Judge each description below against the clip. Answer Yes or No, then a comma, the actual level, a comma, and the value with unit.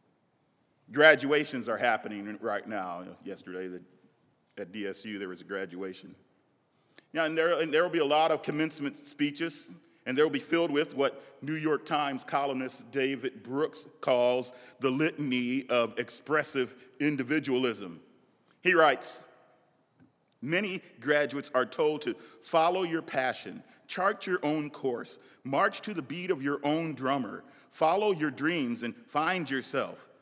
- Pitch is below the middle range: No, medium, 145 Hz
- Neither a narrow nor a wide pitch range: Yes, average, 4.0 semitones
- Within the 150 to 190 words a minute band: No, average, 140 wpm